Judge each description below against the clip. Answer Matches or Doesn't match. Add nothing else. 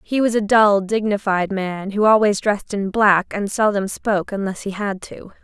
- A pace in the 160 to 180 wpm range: Doesn't match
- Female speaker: Matches